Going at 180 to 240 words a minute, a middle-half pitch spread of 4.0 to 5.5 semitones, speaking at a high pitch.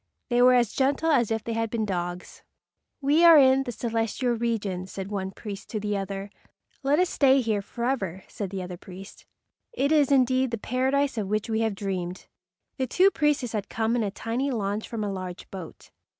Yes: average, 200 wpm; average, 4.9 semitones; high, 225 Hz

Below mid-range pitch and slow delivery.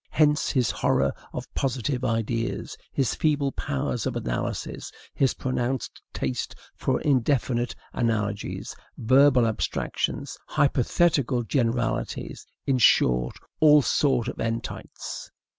Yes: low, 125 Hz; slow, 105 wpm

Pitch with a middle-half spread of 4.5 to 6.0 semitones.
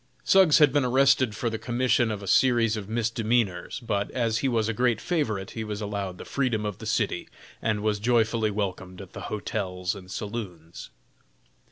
No: average, 3.1 semitones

